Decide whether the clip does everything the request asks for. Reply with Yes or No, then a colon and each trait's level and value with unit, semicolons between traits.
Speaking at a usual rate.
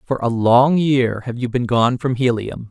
No: fast, 220 wpm